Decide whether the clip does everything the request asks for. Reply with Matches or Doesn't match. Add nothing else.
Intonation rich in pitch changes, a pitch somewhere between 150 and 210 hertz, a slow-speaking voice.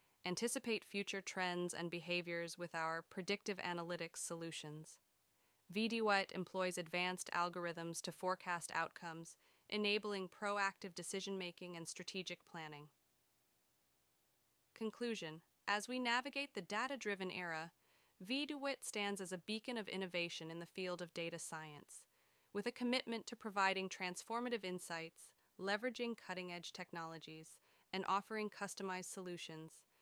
Doesn't match